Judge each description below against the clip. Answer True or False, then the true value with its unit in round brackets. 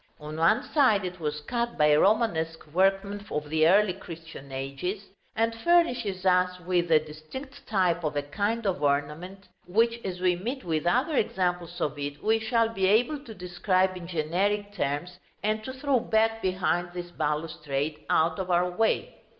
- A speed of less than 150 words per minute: False (170 wpm)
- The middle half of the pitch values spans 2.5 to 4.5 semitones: False (5.1 semitones)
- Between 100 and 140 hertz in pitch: False (180 Hz)